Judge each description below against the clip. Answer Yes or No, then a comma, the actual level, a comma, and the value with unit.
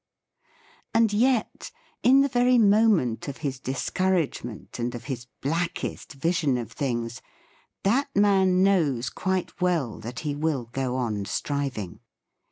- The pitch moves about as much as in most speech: No, wide, 7.8 semitones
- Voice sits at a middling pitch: Yes, medium, 150 Hz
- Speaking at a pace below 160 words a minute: Yes, slow, 135 wpm